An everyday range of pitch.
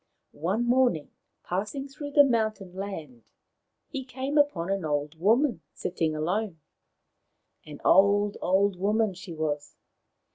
No: wide, 6.6 semitones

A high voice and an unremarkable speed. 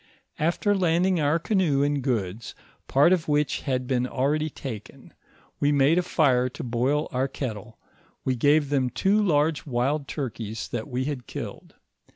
No: medium, 140 Hz; average, 160 wpm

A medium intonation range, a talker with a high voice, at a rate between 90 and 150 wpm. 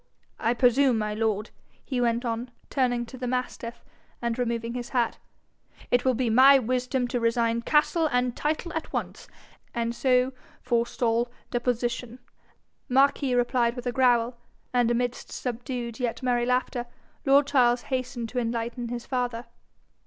No: narrow, 1.4 semitones; high, 245 Hz; average, 145 wpm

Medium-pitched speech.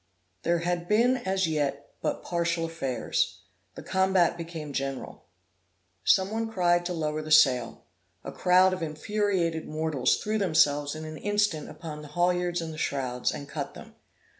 Yes: medium, 165 Hz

